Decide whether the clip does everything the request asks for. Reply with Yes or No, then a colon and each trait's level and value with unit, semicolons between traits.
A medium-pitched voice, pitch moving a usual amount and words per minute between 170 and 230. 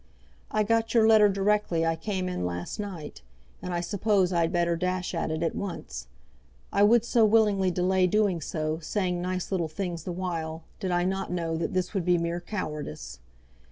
Yes: medium, 180 Hz; average, 3.3 semitones; average, 190 wpm